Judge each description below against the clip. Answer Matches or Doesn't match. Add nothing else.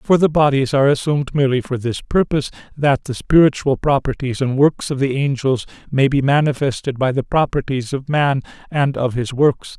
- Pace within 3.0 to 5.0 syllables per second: Doesn't match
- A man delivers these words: Matches